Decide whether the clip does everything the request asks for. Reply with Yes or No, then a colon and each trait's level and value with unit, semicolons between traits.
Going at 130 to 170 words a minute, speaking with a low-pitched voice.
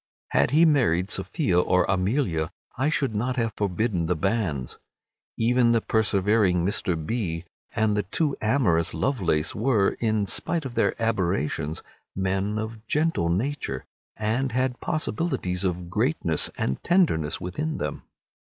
Yes: slow, 135 wpm; low, 105 Hz